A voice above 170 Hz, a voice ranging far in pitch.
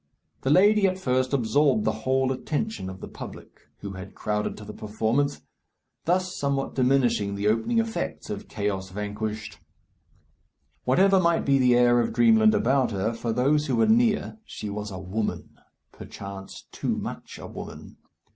No: low, 125 Hz; wide, 6.6 semitones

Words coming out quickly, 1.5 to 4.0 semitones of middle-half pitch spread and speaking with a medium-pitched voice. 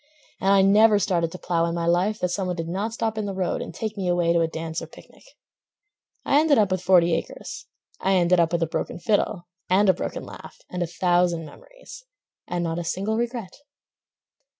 Yes: fast, 220 wpm; average, 3.4 semitones; medium, 180 Hz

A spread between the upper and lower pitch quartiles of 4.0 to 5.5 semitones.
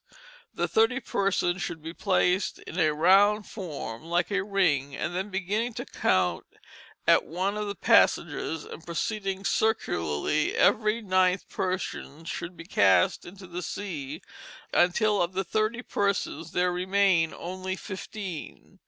No: average, 3.4 semitones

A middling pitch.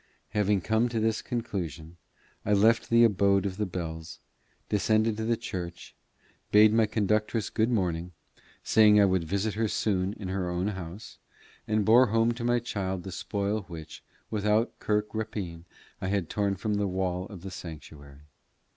No: low, 100 Hz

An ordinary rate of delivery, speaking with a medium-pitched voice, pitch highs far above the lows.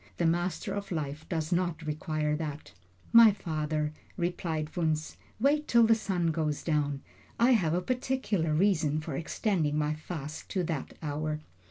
No: average, 155 wpm; medium, 160 Hz; average, 3.5 semitones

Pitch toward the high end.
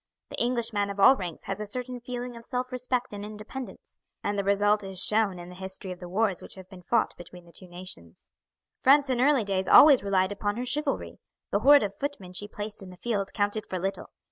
Yes: high, 205 Hz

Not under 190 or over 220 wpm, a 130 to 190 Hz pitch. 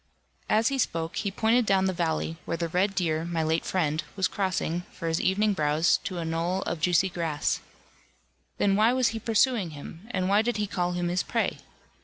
Yes: fast, 205 wpm; medium, 185 Hz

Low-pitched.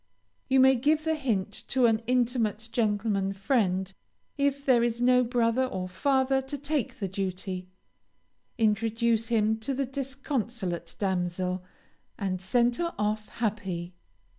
No: high, 230 Hz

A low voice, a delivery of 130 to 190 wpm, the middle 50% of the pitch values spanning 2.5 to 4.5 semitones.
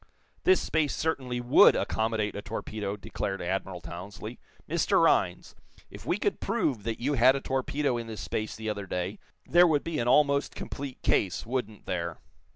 No: low, 115 Hz; average, 170 wpm; average, 5.3 semitones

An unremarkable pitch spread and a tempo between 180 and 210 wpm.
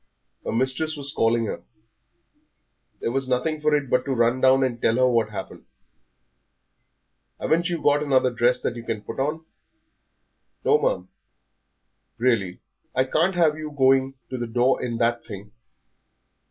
No: average, 3.6 semitones; average, 160 wpm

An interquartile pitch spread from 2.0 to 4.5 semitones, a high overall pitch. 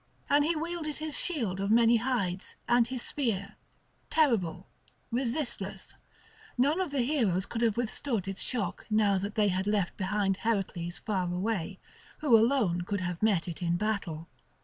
No: average, 5.0 semitones; high, 215 Hz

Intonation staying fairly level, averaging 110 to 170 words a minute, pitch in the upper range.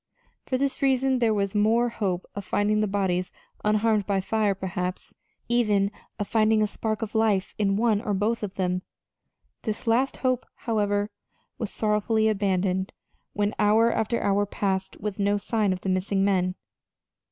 Yes: narrow, 2.1 semitones; average, 165 wpm; high, 210 Hz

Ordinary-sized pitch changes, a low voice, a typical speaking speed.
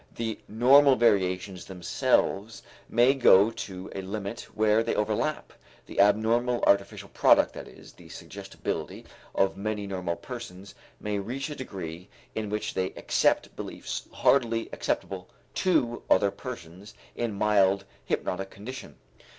No: average, 3.4 semitones; low, 105 Hz; slow, 130 wpm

